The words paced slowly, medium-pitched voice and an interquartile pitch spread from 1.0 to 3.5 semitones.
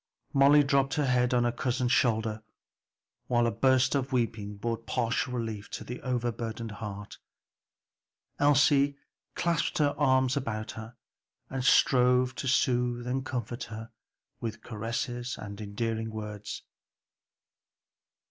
No: slow, 125 wpm; low, 120 Hz; average, 2.7 semitones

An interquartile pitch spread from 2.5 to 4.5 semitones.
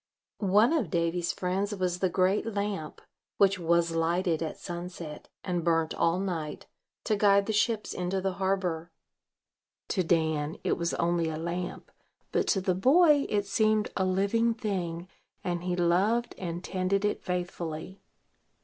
Yes: average, 2.9 semitones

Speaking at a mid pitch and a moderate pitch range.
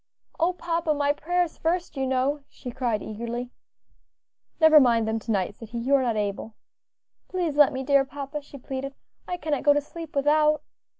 No: very high, 280 Hz; average, 4.0 semitones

